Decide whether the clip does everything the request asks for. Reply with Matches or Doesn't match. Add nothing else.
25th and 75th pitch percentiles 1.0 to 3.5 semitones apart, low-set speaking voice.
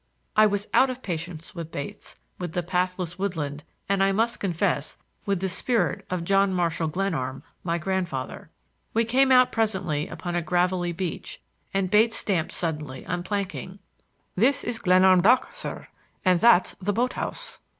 Doesn't match